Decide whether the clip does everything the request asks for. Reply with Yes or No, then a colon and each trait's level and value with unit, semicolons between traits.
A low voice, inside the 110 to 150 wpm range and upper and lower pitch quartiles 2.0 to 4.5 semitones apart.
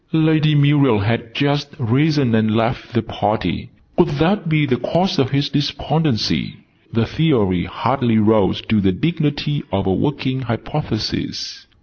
No: low, 130 Hz; average, 140 wpm; average, 5.2 semitones